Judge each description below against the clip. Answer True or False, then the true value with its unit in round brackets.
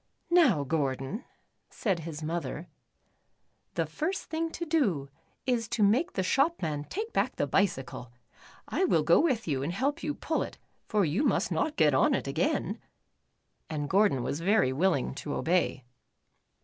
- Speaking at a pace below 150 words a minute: False (160 wpm)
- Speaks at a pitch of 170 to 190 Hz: True (185 Hz)